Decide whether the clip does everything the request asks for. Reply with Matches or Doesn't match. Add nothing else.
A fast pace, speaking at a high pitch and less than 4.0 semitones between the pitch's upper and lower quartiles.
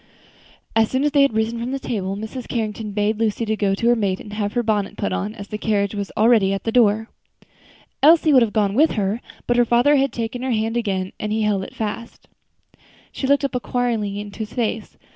Matches